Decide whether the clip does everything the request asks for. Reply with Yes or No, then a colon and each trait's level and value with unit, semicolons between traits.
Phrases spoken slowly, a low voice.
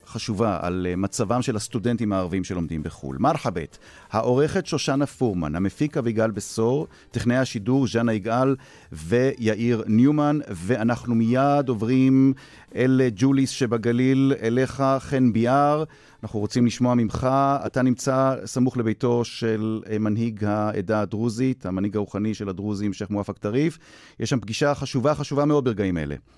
No: average, 130 wpm; low, 120 Hz